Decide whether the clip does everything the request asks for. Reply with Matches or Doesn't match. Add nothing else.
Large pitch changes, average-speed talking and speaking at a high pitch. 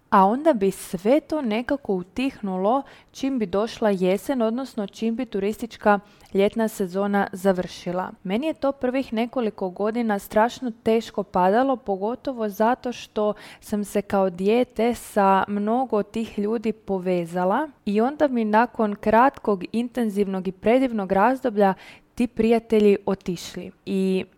Doesn't match